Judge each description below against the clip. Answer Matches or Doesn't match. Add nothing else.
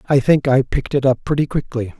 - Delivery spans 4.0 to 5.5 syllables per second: Doesn't match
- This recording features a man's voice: Matches